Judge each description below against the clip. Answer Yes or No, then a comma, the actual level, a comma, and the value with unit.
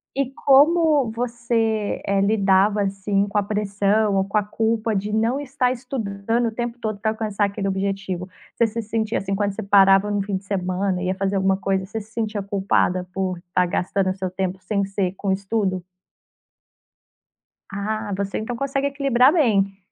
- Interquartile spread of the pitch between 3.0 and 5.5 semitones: No, narrow, 2.6 semitones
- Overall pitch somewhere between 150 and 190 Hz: No, high, 205 Hz